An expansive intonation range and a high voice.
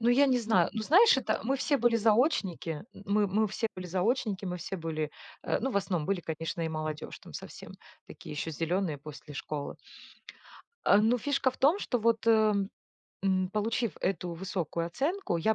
Yes: wide, 5.7 semitones; high, 200 Hz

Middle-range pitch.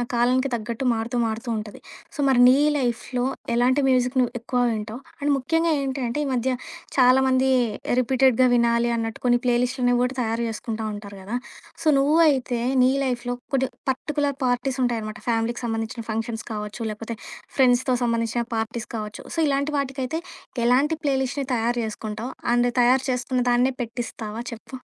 No: high, 245 Hz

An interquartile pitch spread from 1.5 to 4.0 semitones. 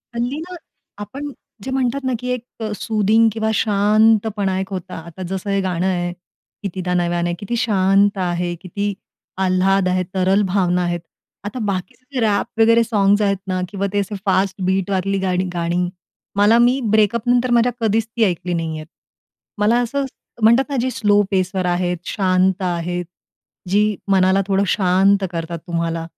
Yes: average, 3.3 semitones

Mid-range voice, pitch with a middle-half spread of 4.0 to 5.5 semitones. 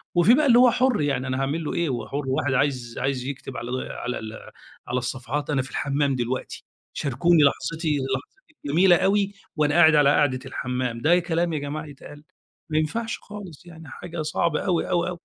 Yes: medium, 150 Hz; average, 4.4 semitones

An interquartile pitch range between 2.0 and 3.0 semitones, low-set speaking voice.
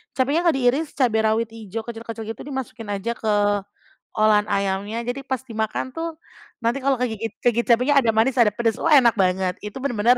No: narrow, 2.6 semitones; high, 230 Hz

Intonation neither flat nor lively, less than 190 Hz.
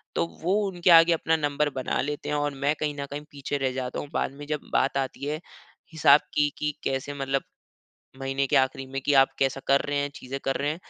No: narrow, 1.7 semitones; medium, 140 Hz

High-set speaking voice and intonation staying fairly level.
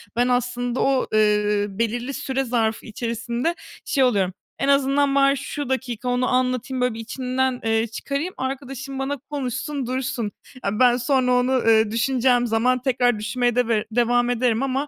Yes: very high, 250 Hz; narrow, 2.3 semitones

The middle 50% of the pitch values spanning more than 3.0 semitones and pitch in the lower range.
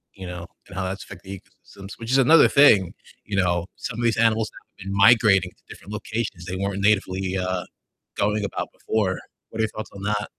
No: average, 2.7 semitones; low, 100 Hz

